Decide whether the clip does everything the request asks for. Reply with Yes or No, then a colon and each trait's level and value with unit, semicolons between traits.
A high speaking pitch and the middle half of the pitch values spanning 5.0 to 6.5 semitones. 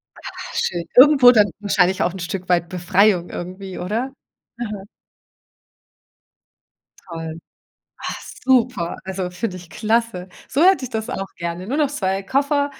Yes: high, 195 Hz; wide, 5.5 semitones